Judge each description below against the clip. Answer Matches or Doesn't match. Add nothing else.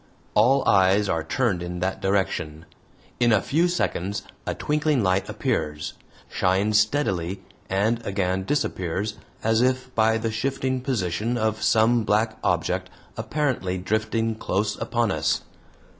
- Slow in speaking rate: Matches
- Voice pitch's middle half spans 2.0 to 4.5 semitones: Matches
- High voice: Doesn't match